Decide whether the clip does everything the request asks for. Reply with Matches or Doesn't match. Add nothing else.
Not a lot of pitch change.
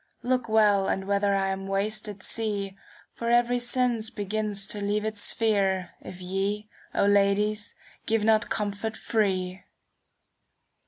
Matches